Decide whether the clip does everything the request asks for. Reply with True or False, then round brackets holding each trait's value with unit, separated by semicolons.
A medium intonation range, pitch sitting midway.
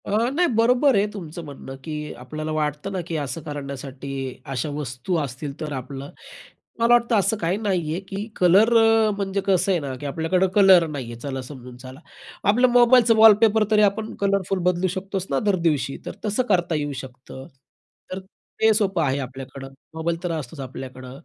False (6.6 semitones; 165 Hz)